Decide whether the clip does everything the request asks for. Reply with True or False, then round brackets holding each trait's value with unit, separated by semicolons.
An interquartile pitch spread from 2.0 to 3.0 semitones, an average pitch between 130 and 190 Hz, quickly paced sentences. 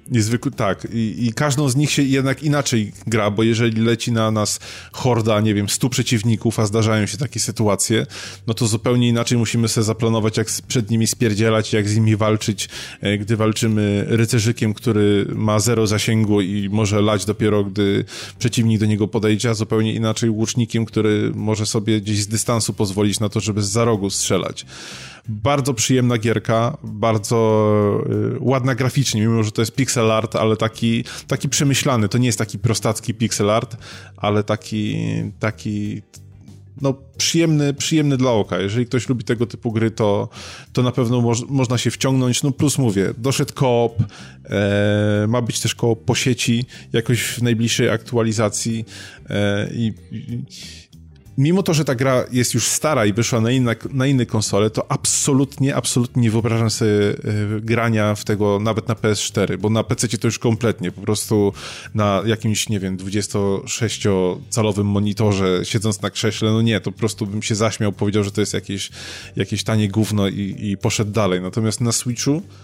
False (2.4 semitones; 110 Hz; 170 wpm)